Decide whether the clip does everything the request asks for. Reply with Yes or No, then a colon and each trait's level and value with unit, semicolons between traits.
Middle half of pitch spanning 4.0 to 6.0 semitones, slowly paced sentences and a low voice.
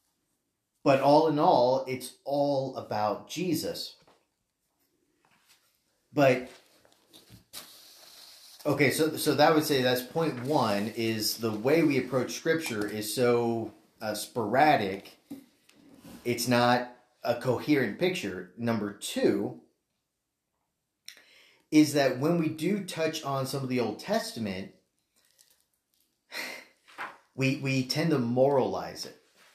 Yes: average, 4.4 semitones; slow, 110 wpm; low, 130 Hz